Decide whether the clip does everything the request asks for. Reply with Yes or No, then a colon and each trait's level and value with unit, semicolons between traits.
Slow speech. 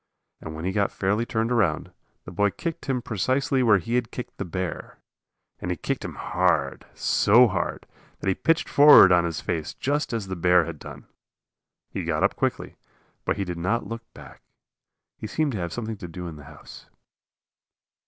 No: average, 195 wpm